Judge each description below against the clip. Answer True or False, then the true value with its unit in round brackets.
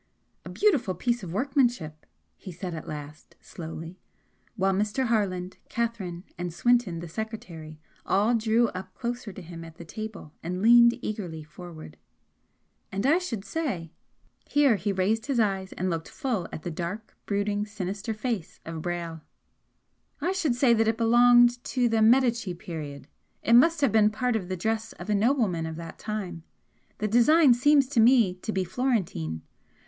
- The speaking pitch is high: True (210 Hz)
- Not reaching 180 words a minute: True (165 wpm)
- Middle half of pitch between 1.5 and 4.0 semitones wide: False (5.4 semitones)